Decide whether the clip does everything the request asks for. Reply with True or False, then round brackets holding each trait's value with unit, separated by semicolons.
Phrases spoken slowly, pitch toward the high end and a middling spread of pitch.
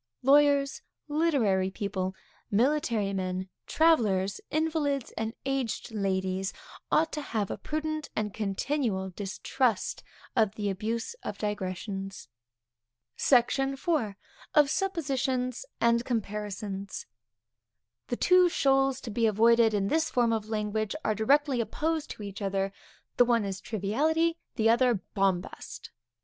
False (120 wpm; 225 Hz; 5.7 semitones)